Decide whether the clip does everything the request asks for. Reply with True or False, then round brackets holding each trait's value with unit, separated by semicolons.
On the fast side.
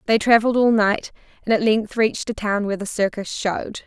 True (215 wpm)